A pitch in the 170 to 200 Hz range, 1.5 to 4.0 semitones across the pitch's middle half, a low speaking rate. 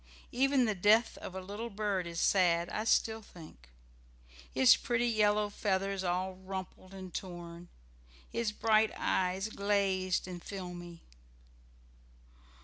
Yes: high, 190 Hz; average, 2.8 semitones; slow, 125 wpm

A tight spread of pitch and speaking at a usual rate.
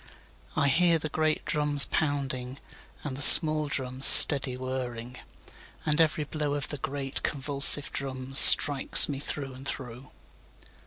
No: narrow, 2.2 semitones; slow, 120 wpm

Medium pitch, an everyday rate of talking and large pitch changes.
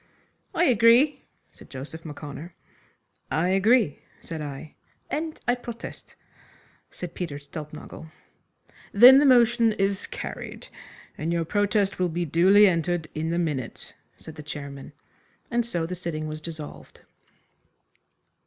No: medium, 170 Hz; slow, 125 wpm; wide, 6.1 semitones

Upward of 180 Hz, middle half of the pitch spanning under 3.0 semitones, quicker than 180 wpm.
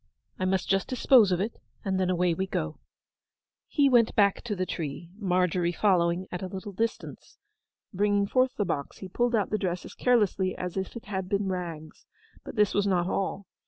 Yes: high, 190 Hz; narrow, 2.5 semitones; average, 195 wpm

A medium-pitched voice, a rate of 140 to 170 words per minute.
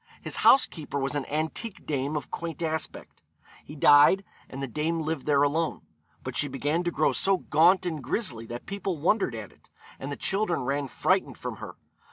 No: medium, 155 Hz; average, 190 wpm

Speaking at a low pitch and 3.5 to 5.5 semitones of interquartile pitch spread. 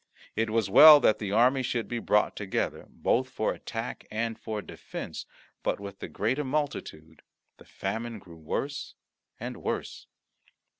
Yes: low, 115 Hz; average, 4.0 semitones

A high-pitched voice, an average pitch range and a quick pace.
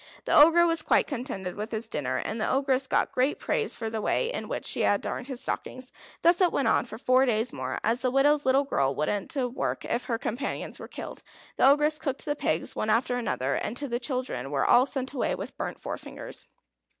Yes: very high, 255 Hz; average, 4.2 semitones; fast, 220 wpm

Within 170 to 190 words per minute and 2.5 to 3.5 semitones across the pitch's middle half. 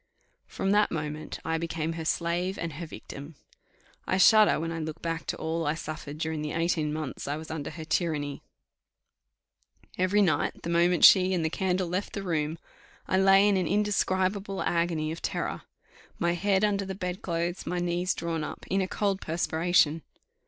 Yes: average, 180 wpm; average, 2.9 semitones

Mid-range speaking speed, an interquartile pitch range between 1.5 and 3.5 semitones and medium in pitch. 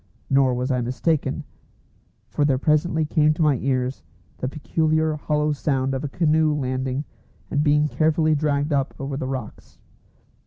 Yes: average, 155 wpm; narrow, 2.6 semitones; medium, 145 Hz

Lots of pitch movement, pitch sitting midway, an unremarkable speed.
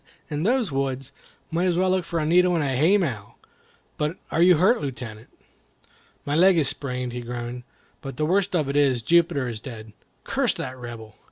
Yes: wide, 5.8 semitones; medium, 145 Hz; average, 190 wpm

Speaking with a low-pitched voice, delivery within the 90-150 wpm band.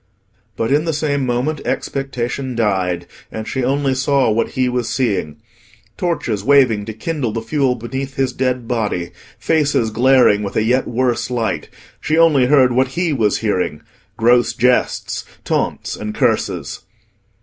Yes: low, 125 Hz; average, 145 wpm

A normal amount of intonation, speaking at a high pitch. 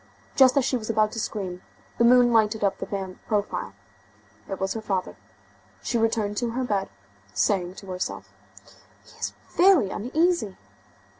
Yes: average, 3.8 semitones; high, 215 Hz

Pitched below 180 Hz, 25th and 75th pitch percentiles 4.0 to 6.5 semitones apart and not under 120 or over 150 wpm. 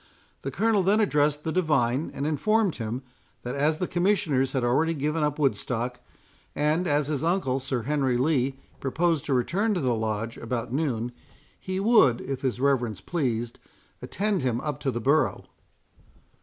No: medium, 140 Hz; average, 4.6 semitones; average, 165 wpm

